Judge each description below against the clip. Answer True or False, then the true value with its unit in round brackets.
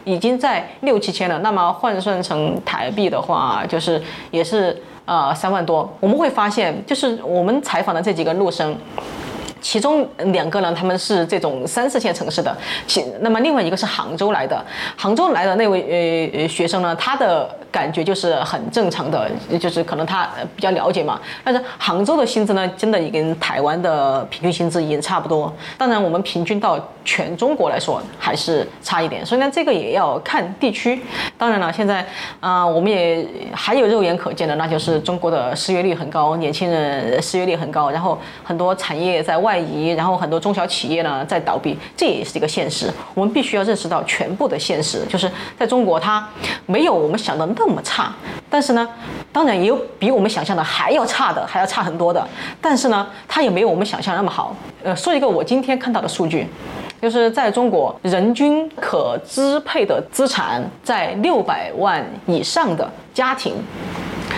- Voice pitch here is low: False (185 Hz)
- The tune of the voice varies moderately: False (5.8 semitones)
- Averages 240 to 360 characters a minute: True (290 characters per minute)